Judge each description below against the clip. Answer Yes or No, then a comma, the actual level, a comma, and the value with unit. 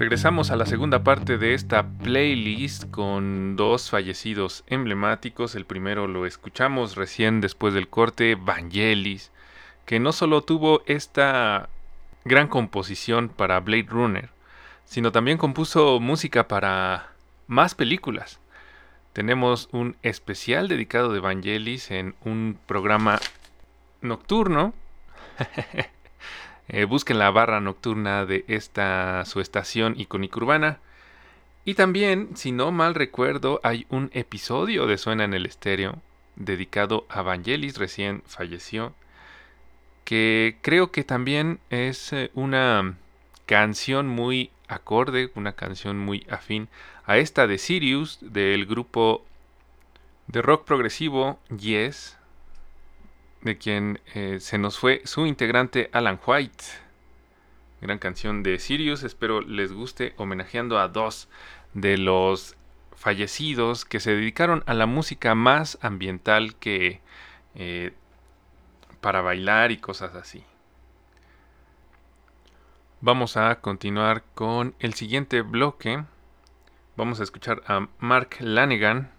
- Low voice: Yes, low, 110 Hz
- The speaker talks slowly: Yes, slow, 115 wpm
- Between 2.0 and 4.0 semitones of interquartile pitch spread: No, average, 4.5 semitones